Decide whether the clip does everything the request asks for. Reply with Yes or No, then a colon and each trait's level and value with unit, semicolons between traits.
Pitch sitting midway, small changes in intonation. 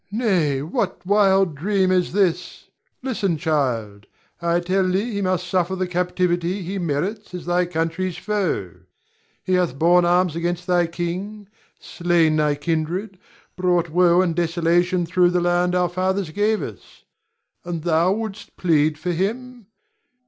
Yes: medium, 180 Hz; narrow, 2.1 semitones